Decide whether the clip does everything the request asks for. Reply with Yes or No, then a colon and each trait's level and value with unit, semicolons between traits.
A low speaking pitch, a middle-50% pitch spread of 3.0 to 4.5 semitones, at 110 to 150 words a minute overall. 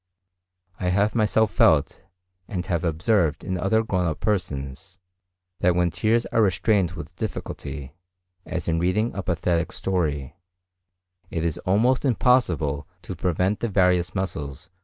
Yes: very low, 90 Hz; average, 3.9 semitones; average, 140 wpm